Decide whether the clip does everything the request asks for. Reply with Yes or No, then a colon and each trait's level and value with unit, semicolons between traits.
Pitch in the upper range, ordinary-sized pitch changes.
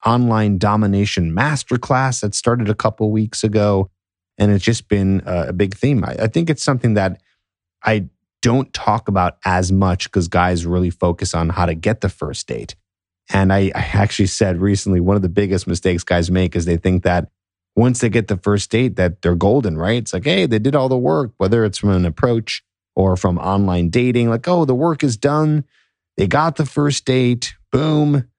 No: low, 100 Hz; average, 4.6 semitones